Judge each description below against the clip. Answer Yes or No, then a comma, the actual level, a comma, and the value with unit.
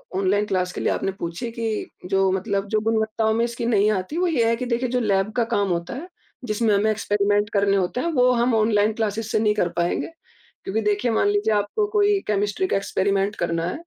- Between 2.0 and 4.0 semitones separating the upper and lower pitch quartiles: Yes, average, 2.8 semitones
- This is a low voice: No, high, 215 Hz